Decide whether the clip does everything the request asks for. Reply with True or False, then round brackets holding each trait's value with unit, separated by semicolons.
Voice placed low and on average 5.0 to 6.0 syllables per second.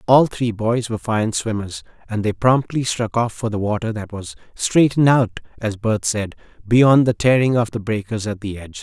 True (110 Hz; 5.1 syllables/s)